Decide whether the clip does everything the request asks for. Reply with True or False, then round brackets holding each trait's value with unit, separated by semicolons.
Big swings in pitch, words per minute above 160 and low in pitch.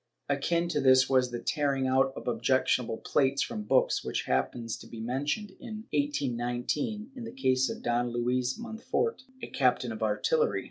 False (3.8 semitones; 170 wpm; 130 Hz)